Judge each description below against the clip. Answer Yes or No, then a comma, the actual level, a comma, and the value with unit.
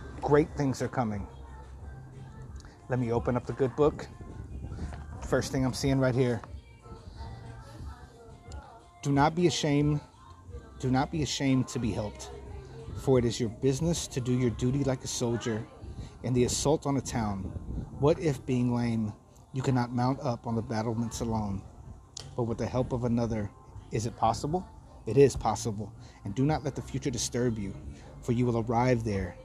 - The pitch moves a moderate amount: Yes, average, 3.7 semitones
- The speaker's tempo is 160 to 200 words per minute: Yes, average, 170 wpm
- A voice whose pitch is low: Yes, low, 120 Hz